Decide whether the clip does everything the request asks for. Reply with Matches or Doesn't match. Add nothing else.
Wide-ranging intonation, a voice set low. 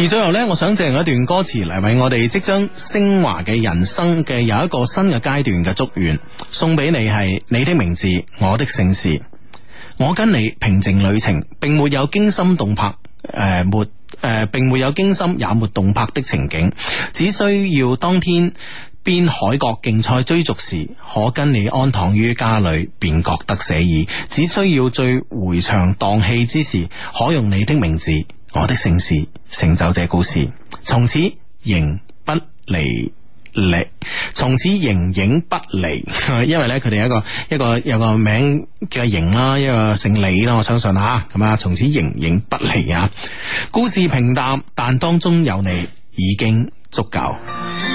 Matches